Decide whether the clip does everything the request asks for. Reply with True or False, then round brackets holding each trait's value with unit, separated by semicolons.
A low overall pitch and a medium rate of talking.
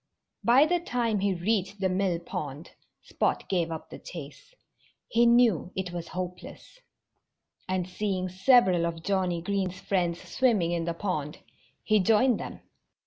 False (185 Hz; 145 wpm)